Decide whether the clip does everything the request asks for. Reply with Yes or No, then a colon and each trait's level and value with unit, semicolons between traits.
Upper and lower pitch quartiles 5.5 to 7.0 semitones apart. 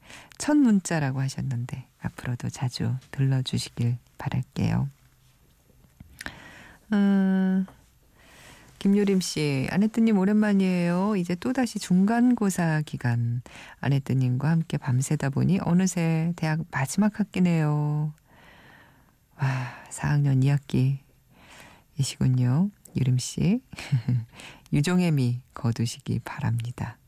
Yes: wide, 6.3 semitones